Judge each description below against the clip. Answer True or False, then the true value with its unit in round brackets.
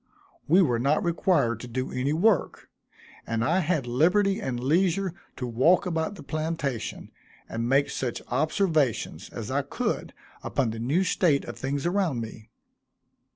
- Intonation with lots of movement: True (6.2 semitones)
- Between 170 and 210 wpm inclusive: False (155 wpm)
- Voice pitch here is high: False (150 Hz)